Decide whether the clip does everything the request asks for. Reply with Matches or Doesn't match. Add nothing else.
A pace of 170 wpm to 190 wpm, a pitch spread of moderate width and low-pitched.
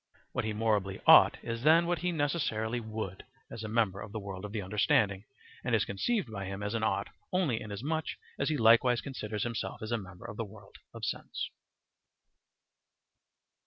Matches